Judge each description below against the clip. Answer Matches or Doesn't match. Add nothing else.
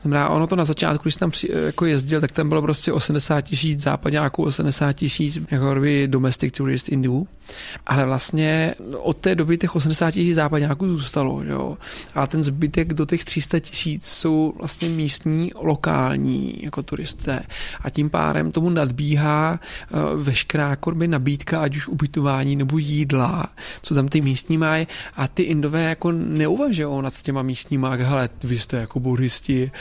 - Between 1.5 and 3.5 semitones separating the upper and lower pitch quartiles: Matches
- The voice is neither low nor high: Matches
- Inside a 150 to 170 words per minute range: Matches